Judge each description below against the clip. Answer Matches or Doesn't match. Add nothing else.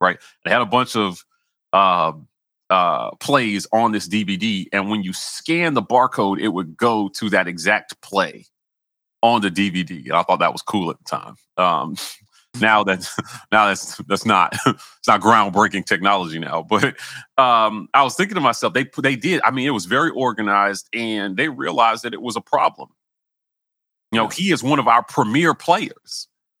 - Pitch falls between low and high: Doesn't match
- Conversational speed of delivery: Matches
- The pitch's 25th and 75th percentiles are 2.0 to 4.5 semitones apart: Matches